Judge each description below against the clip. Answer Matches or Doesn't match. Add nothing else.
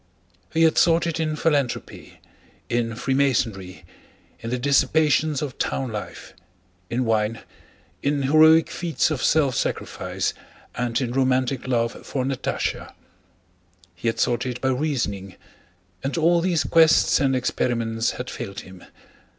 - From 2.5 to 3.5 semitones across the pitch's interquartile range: Doesn't match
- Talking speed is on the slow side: Matches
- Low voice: Matches